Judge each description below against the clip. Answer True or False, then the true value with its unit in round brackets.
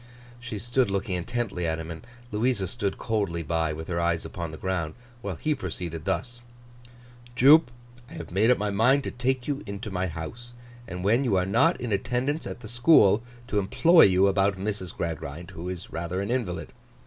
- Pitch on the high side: False (100 Hz)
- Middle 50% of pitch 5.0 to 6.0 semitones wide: True (5.6 semitones)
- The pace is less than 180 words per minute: False (195 wpm)